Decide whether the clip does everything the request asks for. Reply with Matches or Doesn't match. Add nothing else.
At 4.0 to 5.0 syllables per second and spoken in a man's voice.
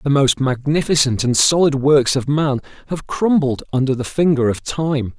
Matches